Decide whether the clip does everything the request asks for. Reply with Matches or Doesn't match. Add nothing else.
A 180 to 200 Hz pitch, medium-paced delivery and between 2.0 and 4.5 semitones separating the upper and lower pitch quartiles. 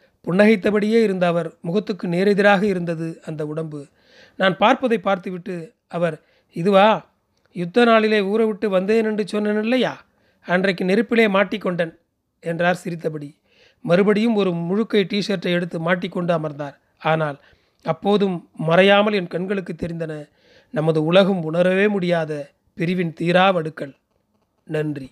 Matches